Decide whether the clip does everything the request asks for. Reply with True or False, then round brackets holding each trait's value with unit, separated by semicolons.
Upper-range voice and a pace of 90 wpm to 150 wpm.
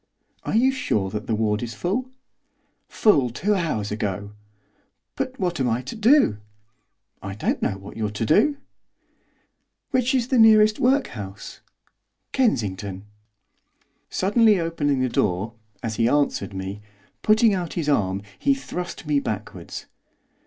False (140 Hz; 140 wpm)